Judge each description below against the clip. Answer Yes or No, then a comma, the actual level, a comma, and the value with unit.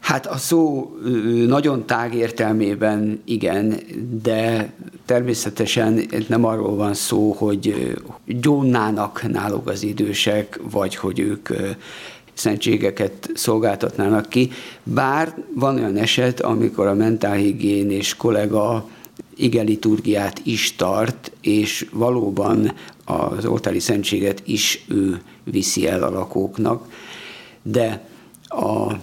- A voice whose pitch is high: No, low, 110 Hz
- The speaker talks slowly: Yes, slow, 100 wpm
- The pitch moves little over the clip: Yes, narrow, 2.3 semitones